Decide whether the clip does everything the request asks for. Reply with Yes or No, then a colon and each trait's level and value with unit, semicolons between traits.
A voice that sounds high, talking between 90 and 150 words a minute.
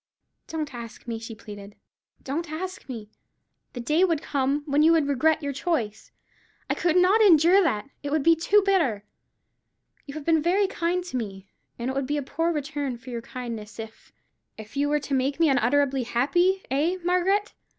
No: very high, 285 Hz; average, 190 wpm